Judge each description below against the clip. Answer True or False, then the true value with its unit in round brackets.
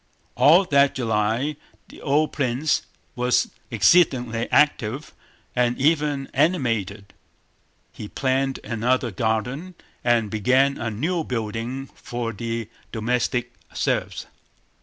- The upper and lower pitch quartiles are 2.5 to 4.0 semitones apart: True (3.6 semitones)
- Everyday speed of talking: False (100 wpm)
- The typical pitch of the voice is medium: False (125 Hz)